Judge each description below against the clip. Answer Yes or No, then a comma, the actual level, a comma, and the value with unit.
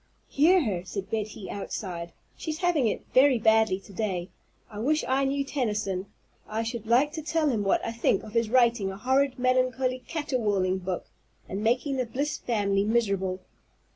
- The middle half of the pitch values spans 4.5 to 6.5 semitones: Yes, average, 4.8 semitones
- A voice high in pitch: Yes, high, 230 Hz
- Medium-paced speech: Yes, average, 170 wpm